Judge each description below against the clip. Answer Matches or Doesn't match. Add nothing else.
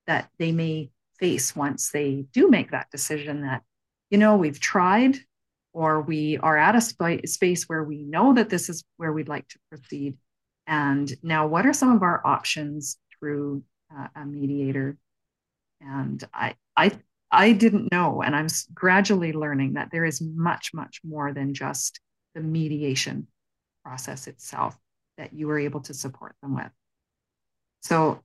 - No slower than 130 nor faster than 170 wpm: Matches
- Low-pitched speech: Doesn't match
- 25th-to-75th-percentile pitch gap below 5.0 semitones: Matches